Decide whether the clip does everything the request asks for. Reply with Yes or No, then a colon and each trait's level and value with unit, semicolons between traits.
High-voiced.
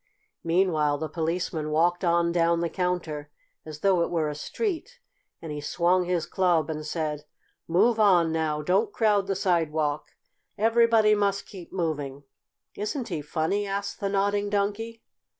No: medium, 175 Hz